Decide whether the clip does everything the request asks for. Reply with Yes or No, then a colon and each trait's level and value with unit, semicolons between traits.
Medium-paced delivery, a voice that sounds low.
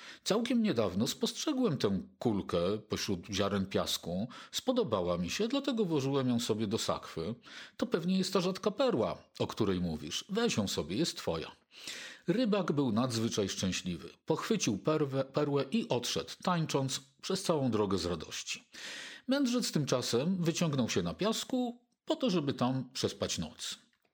No: average, 140 wpm; medium, 160 Hz